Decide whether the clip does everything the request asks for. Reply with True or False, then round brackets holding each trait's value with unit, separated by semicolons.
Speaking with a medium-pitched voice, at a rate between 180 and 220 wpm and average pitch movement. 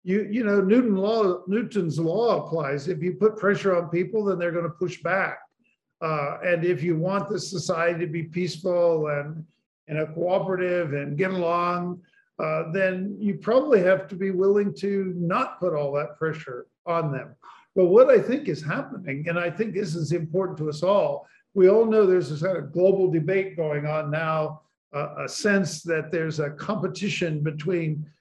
True (180 Hz; 185 wpm; 3.4 semitones)